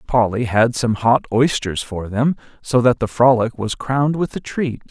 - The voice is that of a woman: No, male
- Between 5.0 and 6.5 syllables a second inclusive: No, 4.6 syllables/s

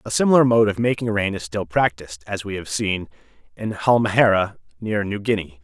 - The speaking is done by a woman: No, male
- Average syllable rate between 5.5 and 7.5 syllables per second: Yes, 5.6 syllables/s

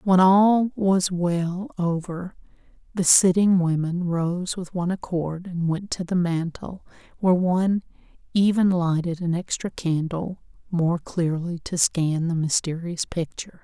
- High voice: No, medium, 175 Hz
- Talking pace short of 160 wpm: Yes, slow, 135 wpm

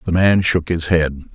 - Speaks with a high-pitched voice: No, very low, 85 Hz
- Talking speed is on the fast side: Yes, fast, 225 wpm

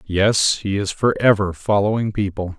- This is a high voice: No, low, 100 Hz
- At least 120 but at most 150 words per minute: Yes, average, 140 wpm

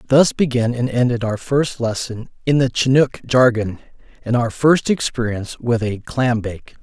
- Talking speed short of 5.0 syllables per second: Yes, 4.6 syllables/s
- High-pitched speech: No, low, 120 Hz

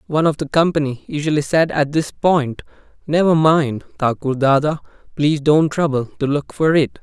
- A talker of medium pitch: Yes, medium, 150 Hz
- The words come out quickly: No, average, 170 wpm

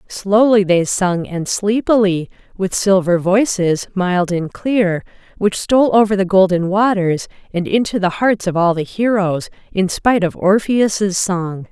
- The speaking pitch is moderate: No, high, 195 Hz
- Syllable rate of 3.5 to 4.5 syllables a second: Yes, 4.1 syllables/s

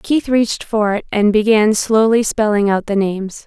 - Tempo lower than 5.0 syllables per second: Yes, 4.8 syllables/s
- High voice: Yes, high, 215 Hz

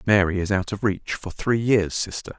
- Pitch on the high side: No, low, 100 Hz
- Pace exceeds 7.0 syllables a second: No, 5.4 syllables/s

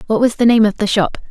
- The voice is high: Yes, high, 215 Hz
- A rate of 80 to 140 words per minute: No, fast, 320 wpm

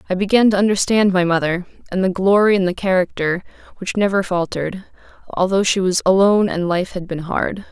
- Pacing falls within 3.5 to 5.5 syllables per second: No, 5.7 syllables/s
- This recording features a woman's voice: Yes, female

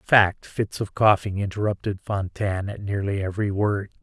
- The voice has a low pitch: Yes, low, 100 Hz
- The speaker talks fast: No, average, 165 wpm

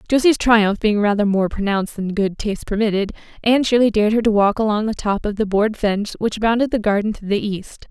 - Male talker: No, female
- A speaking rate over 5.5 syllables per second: Yes, 6.0 syllables/s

